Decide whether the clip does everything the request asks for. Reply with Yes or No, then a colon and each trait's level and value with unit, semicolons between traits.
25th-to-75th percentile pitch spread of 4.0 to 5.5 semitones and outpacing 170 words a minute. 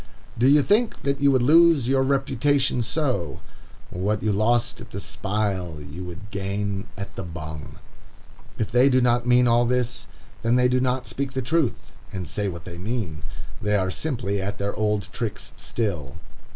Yes: average, 4.7 semitones; average, 180 wpm